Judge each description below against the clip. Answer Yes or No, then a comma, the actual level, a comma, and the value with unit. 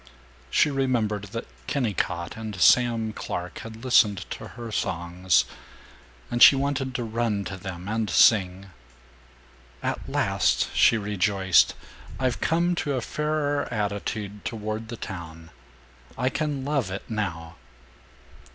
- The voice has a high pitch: No, low, 110 Hz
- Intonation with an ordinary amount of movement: Yes, average, 4.8 semitones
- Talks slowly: Yes, slow, 125 wpm